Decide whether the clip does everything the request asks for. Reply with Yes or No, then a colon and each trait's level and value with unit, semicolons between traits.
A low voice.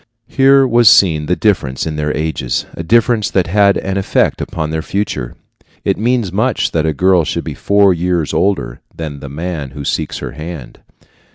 Yes: very low, 85 Hz